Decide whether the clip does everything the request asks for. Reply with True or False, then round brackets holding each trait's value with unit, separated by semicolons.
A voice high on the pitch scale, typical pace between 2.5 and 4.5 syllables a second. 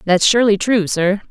False (205 Hz; 5.4 syllables/s)